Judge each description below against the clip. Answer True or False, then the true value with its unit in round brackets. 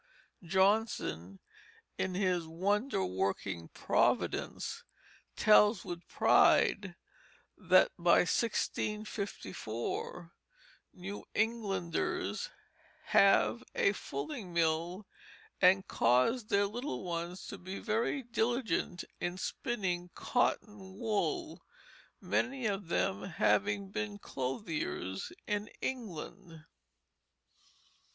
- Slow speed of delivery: True (85 wpm)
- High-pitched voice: True (195 Hz)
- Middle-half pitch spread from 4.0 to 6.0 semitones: True (4.4 semitones)